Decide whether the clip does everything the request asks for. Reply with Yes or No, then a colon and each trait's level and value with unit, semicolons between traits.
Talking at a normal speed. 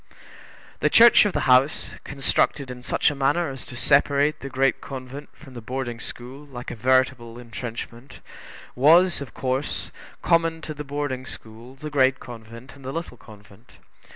Yes: average, 165 wpm